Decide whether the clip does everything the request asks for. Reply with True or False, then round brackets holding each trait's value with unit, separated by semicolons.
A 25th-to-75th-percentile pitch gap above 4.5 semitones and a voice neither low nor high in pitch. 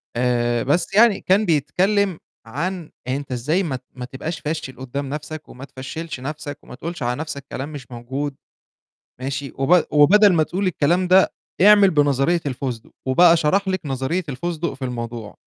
True (4.9 semitones; 145 Hz)